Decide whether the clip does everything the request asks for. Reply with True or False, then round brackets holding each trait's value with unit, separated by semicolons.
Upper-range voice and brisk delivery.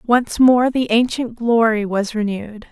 False (230 Hz; 155 wpm)